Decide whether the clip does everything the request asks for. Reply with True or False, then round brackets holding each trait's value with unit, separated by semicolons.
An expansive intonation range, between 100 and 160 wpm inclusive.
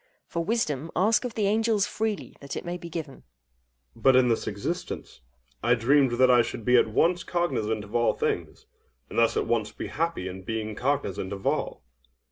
False (7.6 semitones; 195 wpm)